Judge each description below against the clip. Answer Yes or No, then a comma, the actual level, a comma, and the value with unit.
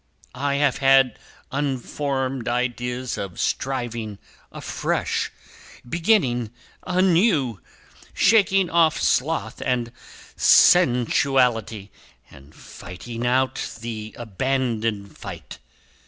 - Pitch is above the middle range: No, low, 125 Hz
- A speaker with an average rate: No, slow, 80 wpm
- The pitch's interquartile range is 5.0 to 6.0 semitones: No, average, 3.4 semitones